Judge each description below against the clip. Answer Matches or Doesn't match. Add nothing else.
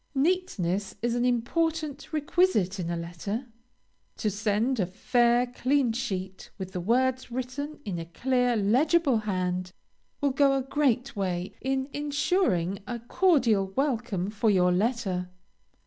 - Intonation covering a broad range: Matches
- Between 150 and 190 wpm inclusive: Doesn't match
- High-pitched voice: Matches